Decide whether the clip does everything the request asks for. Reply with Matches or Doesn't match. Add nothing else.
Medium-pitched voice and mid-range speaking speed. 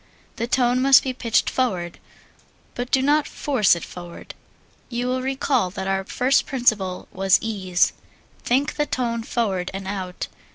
Doesn't match